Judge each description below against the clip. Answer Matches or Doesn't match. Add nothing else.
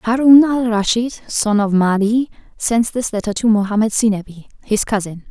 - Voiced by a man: Doesn't match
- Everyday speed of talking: Matches